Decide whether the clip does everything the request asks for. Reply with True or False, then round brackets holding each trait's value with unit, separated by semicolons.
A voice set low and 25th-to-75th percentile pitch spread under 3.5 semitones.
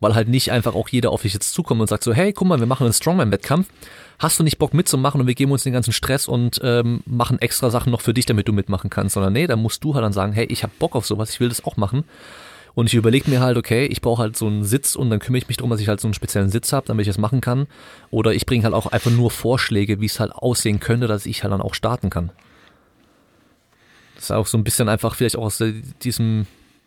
True (115 Hz; 2.8 semitones)